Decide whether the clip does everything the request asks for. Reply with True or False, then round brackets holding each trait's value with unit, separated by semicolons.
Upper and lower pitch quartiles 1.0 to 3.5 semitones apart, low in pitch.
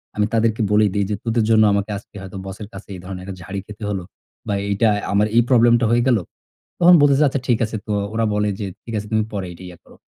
True (2.5 semitones; 105 Hz)